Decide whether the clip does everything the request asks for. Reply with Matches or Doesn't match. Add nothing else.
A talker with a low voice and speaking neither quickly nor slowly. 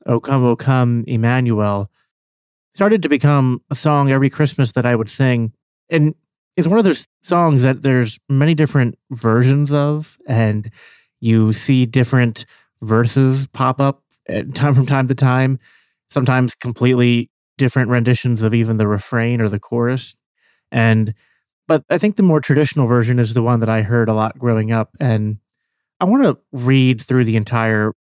Matches